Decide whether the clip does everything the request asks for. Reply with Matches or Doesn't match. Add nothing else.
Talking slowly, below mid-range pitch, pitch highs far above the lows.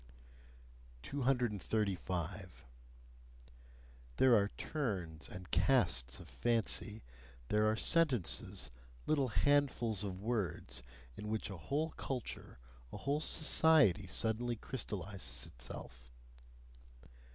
Matches